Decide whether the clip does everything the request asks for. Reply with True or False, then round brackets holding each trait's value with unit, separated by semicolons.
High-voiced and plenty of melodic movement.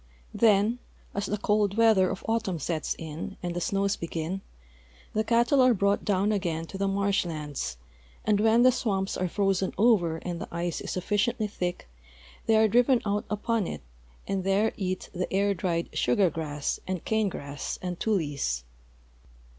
False (195 Hz; 3.7 semitones)